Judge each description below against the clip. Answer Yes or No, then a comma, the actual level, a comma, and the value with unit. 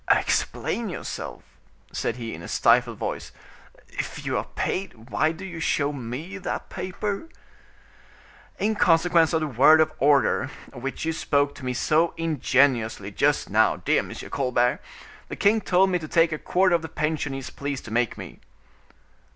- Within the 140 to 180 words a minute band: Yes, average, 170 wpm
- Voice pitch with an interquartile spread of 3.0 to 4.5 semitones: No, average, 5.1 semitones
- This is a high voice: No, medium, 155 Hz